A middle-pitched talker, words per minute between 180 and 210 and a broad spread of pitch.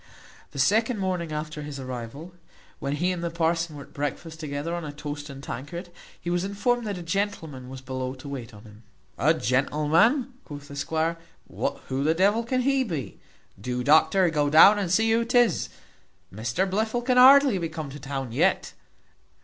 Yes: medium, 160 Hz; average, 185 wpm; wide, 5.7 semitones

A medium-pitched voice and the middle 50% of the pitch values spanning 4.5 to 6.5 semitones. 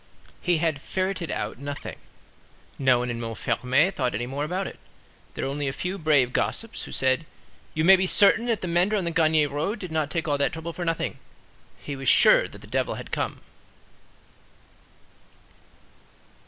Yes: medium, 155 Hz; average, 5.0 semitones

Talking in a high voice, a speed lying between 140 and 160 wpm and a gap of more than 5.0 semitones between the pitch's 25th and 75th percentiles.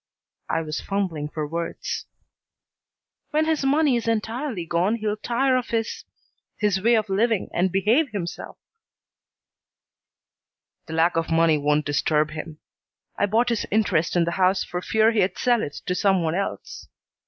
Yes: high, 195 Hz; average, 155 wpm; wide, 5.5 semitones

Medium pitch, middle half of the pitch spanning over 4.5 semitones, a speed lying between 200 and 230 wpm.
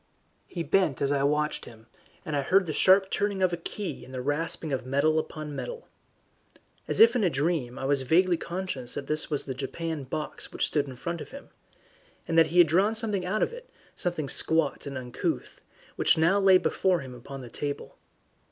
Yes: medium, 160 Hz; average, 5.0 semitones; fast, 205 wpm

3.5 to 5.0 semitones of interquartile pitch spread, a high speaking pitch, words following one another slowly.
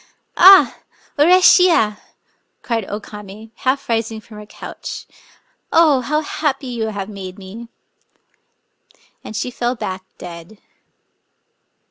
Yes: average, 4.7 semitones; high, 225 Hz; slow, 130 wpm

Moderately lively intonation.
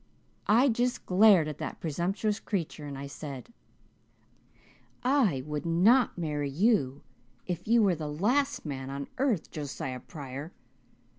No: wide, 7.4 semitones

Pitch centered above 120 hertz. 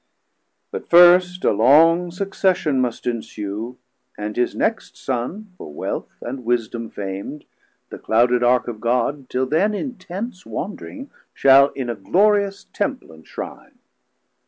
Yes: low, 135 Hz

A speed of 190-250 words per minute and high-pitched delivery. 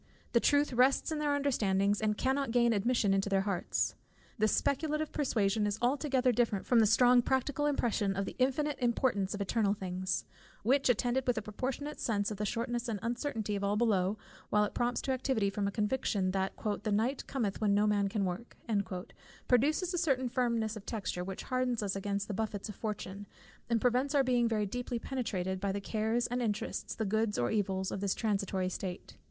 Yes: average, 195 wpm; high, 220 Hz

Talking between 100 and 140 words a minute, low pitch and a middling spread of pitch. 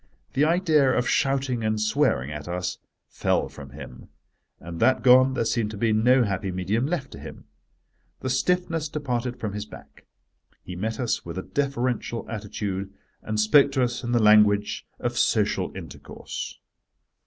No: average, 165 wpm; low, 115 Hz; average, 4.4 semitones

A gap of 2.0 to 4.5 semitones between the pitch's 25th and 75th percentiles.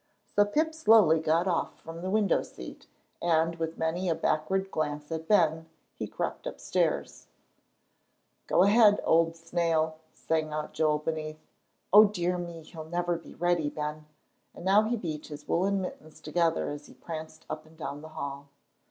Yes: narrow, 2.4 semitones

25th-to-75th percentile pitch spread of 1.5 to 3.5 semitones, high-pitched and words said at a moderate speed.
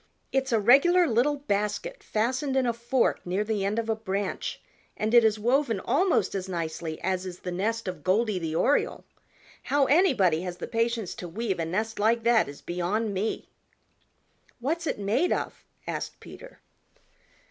No: average, 5.0 semitones; high, 220 Hz; average, 170 wpm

